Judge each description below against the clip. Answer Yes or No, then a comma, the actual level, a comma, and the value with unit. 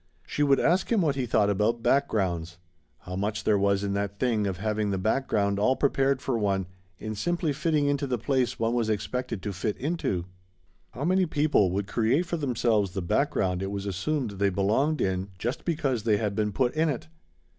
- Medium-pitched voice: No, low, 110 Hz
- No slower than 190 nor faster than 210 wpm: Yes, average, 200 wpm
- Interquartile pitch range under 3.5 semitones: No, wide, 5.6 semitones